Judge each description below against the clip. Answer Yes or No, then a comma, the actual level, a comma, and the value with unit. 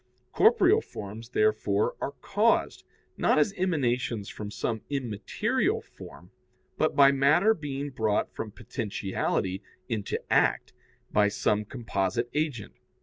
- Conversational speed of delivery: No, slow, 115 wpm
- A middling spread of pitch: No, wide, 6.6 semitones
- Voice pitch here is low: Yes, low, 120 Hz